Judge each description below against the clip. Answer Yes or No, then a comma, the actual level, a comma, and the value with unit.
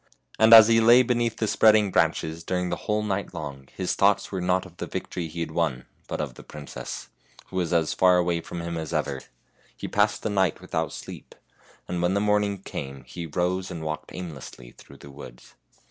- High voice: No, very low, 90 Hz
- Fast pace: Yes, fast, 210 wpm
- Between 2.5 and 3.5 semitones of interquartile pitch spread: No, average, 4.4 semitones